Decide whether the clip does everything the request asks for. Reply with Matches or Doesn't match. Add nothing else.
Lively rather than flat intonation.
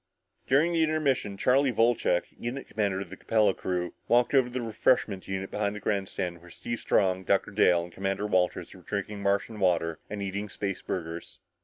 Doesn't match